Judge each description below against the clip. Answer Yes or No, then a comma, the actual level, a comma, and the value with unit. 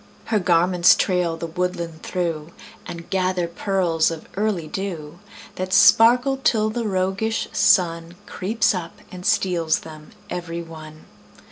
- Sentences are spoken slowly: Yes, slow, 130 wpm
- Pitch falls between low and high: Yes, medium, 180 Hz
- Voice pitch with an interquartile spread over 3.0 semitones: No, narrow, 2.6 semitones